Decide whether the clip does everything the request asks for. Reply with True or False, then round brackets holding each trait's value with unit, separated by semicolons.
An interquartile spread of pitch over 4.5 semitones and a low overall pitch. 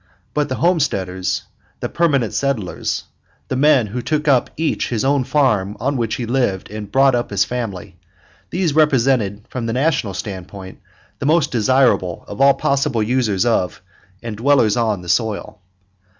True (5.0 semitones; 120 Hz)